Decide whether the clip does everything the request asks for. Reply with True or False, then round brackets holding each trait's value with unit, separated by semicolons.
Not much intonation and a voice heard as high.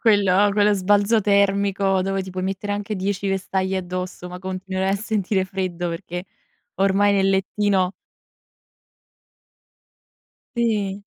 True (1.4 semitones; 195 Hz)